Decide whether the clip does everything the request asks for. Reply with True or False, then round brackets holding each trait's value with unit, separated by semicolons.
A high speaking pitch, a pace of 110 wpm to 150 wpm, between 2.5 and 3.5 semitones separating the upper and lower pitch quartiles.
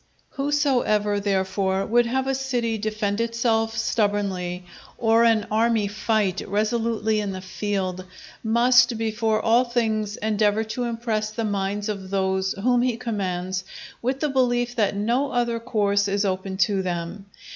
True (215 Hz; 145 wpm; 2.8 semitones)